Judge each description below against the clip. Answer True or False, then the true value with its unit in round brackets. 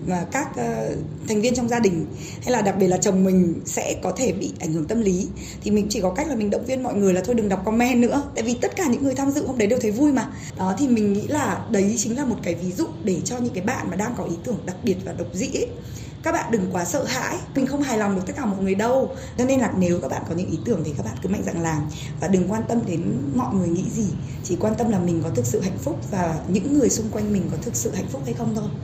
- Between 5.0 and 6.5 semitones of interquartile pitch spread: True (5.5 semitones)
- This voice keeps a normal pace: False (310 wpm)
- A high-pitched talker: True (200 Hz)